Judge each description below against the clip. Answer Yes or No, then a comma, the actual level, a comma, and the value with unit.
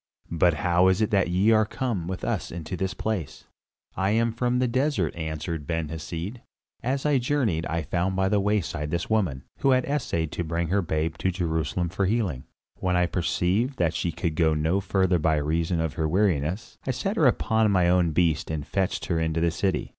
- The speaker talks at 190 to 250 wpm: Yes, fast, 205 wpm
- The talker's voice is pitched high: No, very low, 90 Hz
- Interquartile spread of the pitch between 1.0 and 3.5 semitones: No, average, 4.5 semitones